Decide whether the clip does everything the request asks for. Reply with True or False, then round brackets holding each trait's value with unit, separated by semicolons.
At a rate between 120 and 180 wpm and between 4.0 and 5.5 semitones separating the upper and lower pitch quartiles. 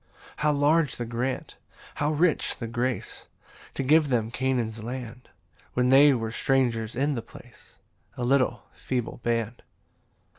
False (145 wpm; 3.0 semitones)